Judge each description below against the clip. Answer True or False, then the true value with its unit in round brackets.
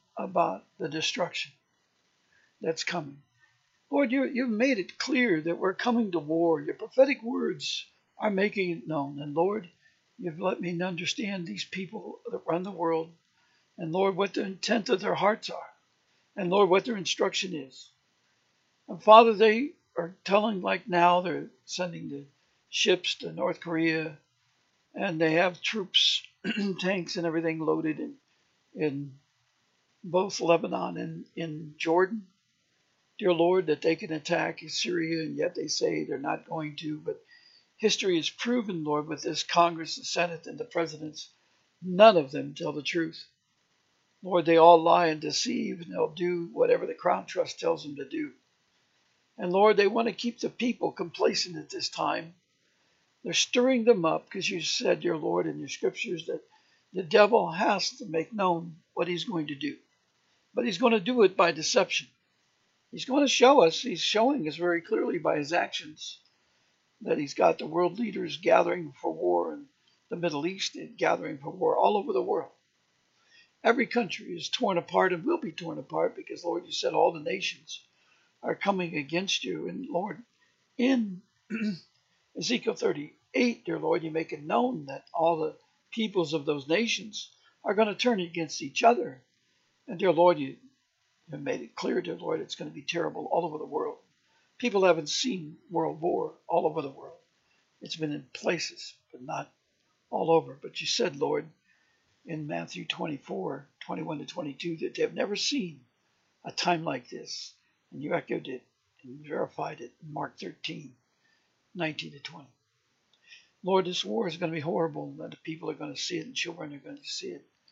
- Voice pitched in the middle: True (180 Hz)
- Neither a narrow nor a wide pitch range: False (6.3 semitones)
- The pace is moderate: True (175 wpm)